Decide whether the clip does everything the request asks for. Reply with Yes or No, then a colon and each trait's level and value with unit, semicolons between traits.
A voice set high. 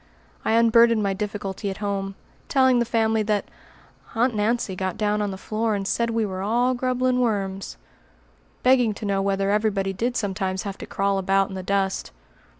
Yes: high, 210 Hz